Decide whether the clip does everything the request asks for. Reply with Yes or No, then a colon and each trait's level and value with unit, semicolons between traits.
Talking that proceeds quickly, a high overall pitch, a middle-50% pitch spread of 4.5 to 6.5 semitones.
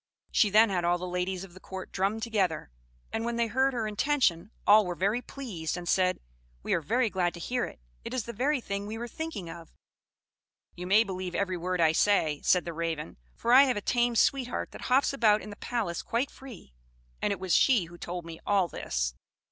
Yes: fast, 220 wpm; high, 200 Hz; average, 5.1 semitones